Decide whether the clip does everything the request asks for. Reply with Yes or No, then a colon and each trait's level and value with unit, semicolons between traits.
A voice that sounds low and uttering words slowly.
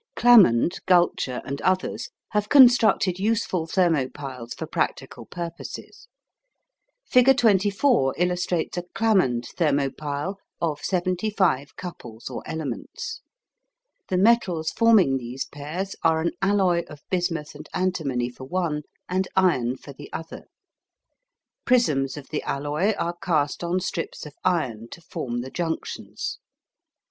No: medium, 170 Hz; slow, 125 wpm